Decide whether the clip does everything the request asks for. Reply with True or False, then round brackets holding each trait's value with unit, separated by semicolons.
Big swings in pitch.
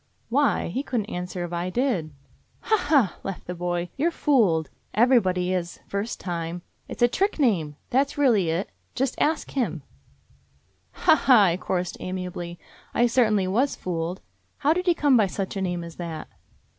True (6.8 semitones)